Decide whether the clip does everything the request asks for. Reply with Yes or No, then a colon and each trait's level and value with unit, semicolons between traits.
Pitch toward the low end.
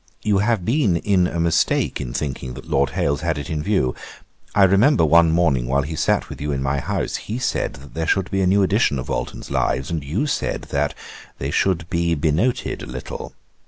Yes: very low, 85 Hz